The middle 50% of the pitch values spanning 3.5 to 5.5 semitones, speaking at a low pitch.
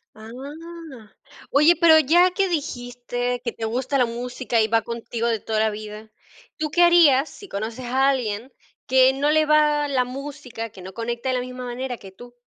No: average, 4.2 semitones; very high, 250 Hz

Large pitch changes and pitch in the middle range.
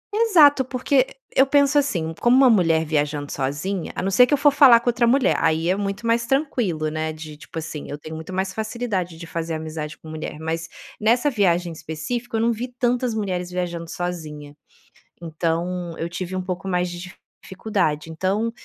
Yes: wide, 6.6 semitones; medium, 180 Hz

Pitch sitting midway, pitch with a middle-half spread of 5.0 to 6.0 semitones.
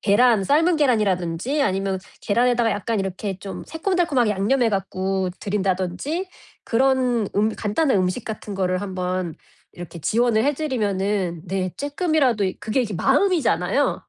No: high, 210 Hz; wide, 5.5 semitones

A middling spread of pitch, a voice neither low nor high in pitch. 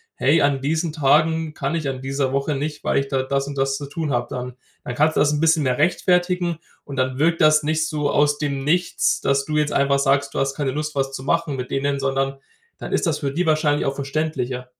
No: narrow, 2.2 semitones; medium, 145 Hz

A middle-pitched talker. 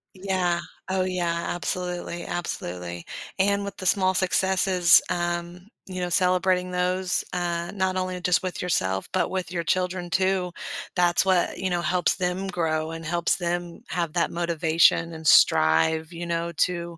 Yes: medium, 175 Hz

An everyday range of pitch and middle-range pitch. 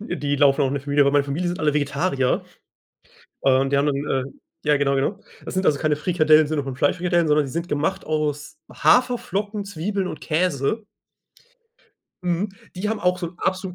Yes: average, 4.3 semitones; medium, 155 Hz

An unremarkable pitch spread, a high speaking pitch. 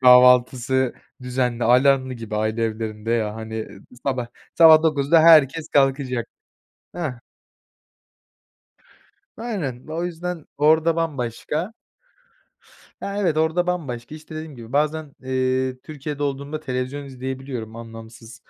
No: average, 4.3 semitones; low, 135 Hz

